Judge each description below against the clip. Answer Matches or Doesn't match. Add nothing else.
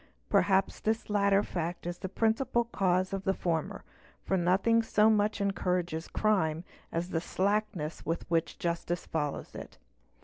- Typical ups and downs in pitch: Matches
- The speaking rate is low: Doesn't match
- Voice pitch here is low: Doesn't match